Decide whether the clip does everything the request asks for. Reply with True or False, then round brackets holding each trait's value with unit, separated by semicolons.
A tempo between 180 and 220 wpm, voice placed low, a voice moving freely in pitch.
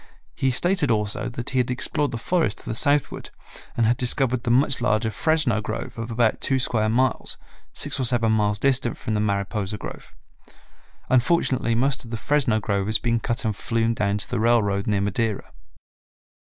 False (185 wpm; 115 Hz; 2.9 semitones)